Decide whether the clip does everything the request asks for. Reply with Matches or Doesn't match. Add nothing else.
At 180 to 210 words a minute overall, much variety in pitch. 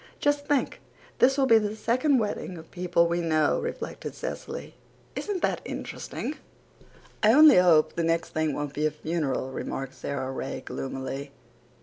Doesn't match